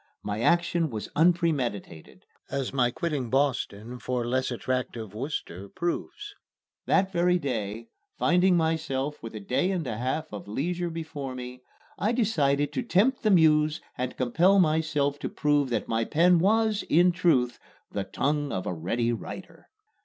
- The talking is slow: No, average, 155 wpm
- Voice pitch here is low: No, medium, 145 Hz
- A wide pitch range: Yes, wide, 5.9 semitones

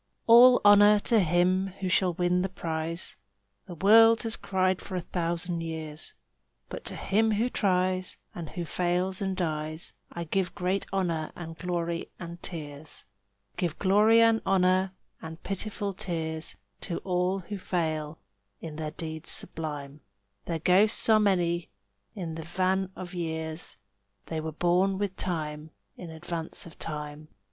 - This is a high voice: No, medium, 175 Hz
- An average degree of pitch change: Yes, average, 3.0 semitones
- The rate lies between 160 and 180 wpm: No, average, 150 wpm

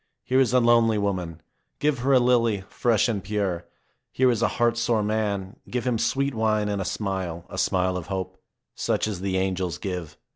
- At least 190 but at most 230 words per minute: Yes, average, 195 wpm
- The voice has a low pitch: Yes, low, 105 Hz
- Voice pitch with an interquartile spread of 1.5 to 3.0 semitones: No, average, 4.0 semitones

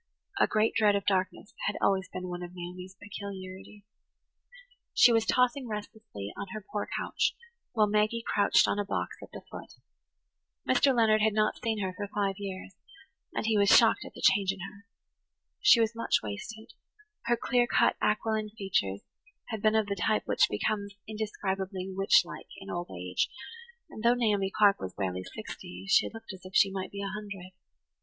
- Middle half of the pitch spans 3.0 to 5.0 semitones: No, narrow, 2.4 semitones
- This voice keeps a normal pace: Yes, average, 185 wpm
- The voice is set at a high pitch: Yes, high, 205 Hz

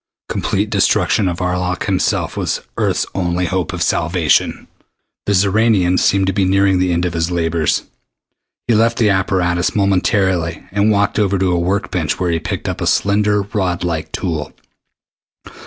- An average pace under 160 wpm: No, average, 165 wpm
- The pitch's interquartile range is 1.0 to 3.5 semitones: Yes, narrow, 2.4 semitones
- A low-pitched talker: Yes, very low, 90 Hz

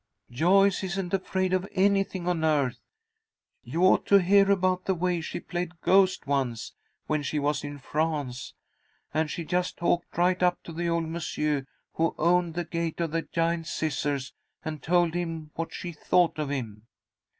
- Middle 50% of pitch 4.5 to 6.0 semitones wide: No, average, 2.8 semitones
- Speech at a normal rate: Yes, average, 170 wpm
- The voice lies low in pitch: No, medium, 170 Hz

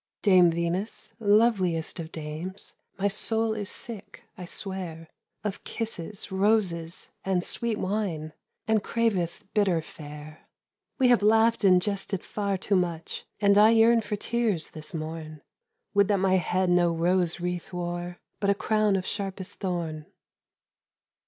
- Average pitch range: Yes, average, 3.6 semitones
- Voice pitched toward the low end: No, high, 190 Hz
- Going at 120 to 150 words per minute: Yes, average, 140 wpm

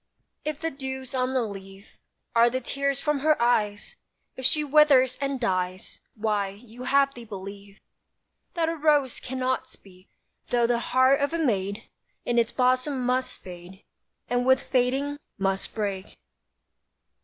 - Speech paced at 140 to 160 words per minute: Yes, average, 150 wpm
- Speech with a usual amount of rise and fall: Yes, average, 5.0 semitones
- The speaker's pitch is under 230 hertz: No, very high, 250 Hz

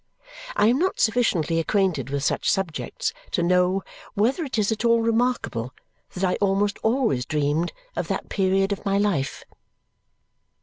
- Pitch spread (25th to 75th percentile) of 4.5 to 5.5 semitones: Yes, average, 5.2 semitones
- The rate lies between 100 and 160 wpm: Yes, average, 155 wpm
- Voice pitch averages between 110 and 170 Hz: No, high, 195 Hz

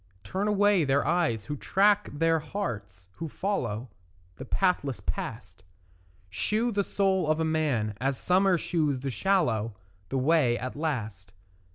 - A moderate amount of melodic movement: No, wide, 7.8 semitones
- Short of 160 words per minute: Yes, average, 140 wpm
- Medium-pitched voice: Yes, medium, 155 Hz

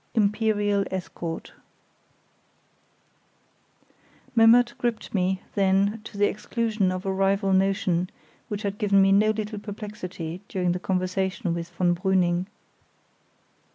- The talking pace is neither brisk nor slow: No, slow, 115 wpm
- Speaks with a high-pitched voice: Yes, high, 195 Hz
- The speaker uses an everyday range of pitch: No, narrow, 2.3 semitones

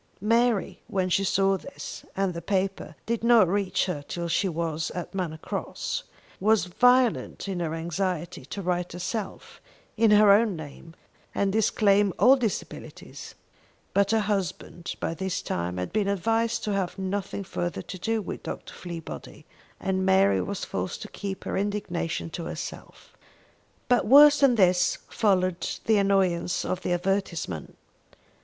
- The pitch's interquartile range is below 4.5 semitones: Yes, average, 2.9 semitones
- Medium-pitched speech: No, high, 195 Hz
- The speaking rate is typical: Yes, average, 150 wpm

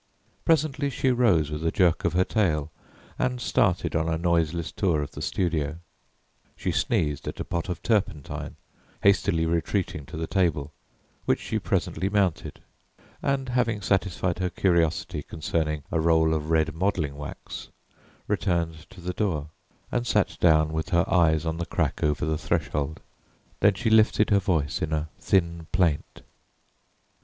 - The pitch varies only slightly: No, average, 3.7 semitones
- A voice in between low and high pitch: No, very low, 85 Hz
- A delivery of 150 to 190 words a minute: Yes, average, 155 wpm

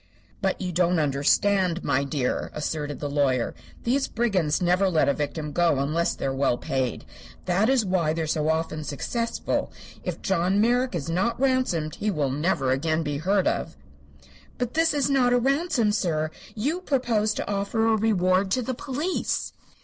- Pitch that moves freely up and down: Yes, wide, 7.2 semitones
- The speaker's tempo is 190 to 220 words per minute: No, average, 180 wpm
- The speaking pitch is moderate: Yes, medium, 180 Hz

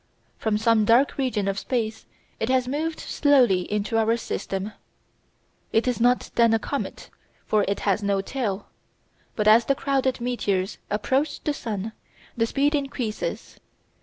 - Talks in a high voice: Yes, high, 230 Hz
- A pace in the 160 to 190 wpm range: No, average, 150 wpm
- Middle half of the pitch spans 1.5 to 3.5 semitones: No, average, 3.9 semitones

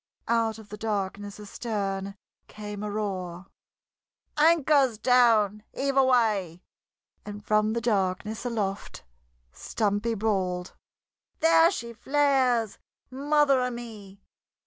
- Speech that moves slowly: Yes, slow, 100 wpm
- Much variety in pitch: No, average, 3.7 semitones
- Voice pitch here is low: No, high, 215 Hz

